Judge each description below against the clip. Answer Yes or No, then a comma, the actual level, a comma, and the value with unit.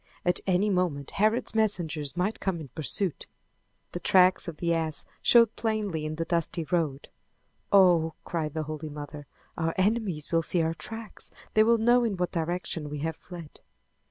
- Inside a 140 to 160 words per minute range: No, average, 170 wpm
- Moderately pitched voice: Yes, medium, 170 Hz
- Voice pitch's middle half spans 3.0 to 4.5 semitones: Yes, average, 4.1 semitones